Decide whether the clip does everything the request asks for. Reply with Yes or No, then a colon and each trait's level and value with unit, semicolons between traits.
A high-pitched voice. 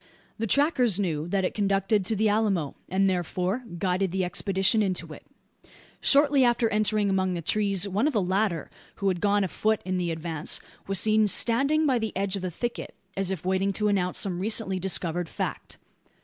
Yes: high, 195 Hz